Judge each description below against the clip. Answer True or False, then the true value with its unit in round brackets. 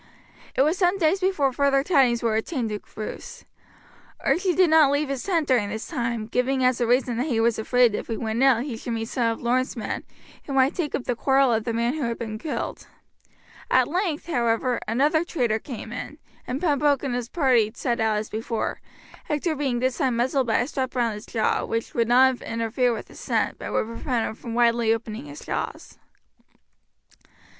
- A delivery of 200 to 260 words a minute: True (205 wpm)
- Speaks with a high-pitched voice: True (250 Hz)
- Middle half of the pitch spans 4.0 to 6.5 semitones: False (3.5 semitones)